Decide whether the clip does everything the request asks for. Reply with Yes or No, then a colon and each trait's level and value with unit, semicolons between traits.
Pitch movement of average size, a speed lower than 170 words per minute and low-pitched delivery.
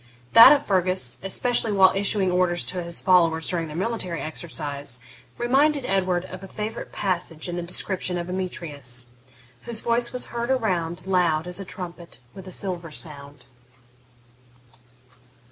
No: average, 3.0 semitones; average, 145 wpm; medium, 180 Hz